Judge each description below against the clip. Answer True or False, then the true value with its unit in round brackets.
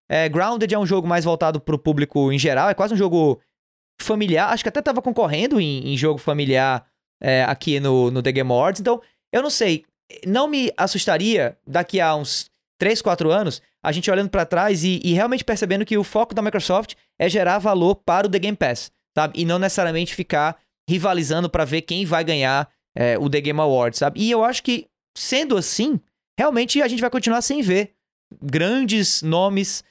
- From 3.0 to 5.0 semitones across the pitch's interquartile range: False (5.6 semitones)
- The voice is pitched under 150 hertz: False (180 Hz)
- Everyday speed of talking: False (205 wpm)